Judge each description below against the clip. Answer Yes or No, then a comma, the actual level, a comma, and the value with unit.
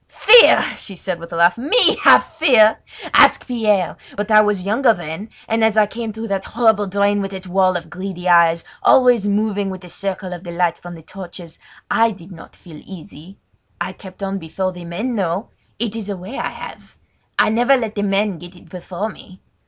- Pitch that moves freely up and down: No, average, 3.5 semitones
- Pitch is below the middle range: No, high, 195 Hz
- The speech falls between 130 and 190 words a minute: No, fast, 205 wpm